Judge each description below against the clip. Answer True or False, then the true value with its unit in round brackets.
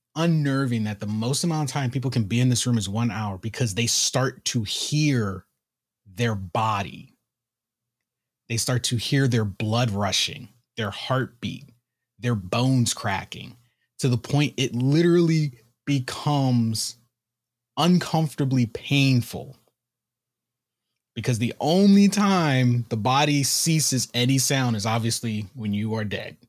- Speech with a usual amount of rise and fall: True (3.4 semitones)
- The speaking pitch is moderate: False (120 Hz)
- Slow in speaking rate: True (130 wpm)